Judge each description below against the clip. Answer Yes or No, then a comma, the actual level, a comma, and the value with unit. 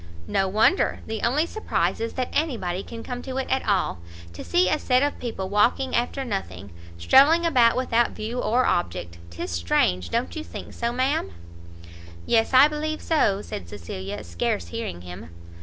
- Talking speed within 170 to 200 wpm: Yes, average, 175 wpm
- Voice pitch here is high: Yes, high, 230 Hz